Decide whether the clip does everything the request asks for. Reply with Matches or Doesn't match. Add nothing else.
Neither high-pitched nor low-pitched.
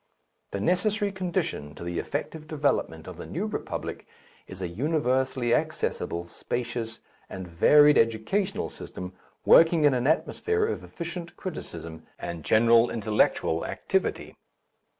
Doesn't match